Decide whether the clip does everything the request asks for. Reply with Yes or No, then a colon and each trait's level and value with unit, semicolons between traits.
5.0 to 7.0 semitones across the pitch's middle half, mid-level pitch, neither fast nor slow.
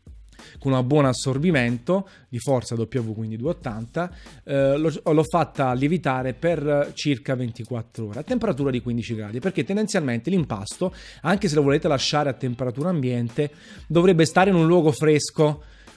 Yes: average, 5.3 semitones; medium, 145 Hz; average, 150 wpm